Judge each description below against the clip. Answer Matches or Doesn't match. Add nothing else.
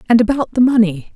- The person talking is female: Matches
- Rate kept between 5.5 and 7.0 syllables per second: Matches